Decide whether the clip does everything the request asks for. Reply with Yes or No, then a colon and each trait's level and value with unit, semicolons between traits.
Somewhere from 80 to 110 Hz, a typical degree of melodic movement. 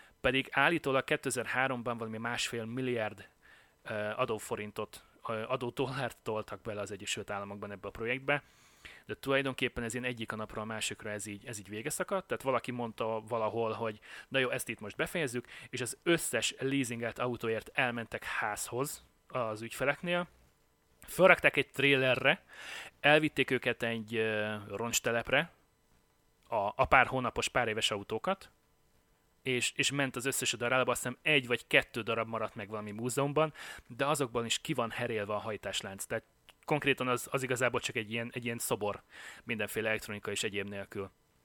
No: low, 120 Hz; average, 3.5 semitones